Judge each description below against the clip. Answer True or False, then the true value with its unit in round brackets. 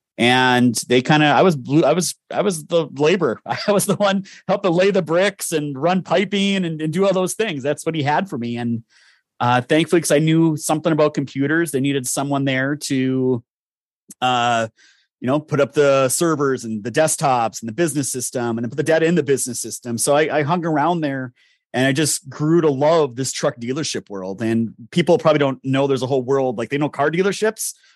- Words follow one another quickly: True (220 wpm)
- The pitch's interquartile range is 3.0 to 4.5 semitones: True (4.2 semitones)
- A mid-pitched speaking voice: True (145 Hz)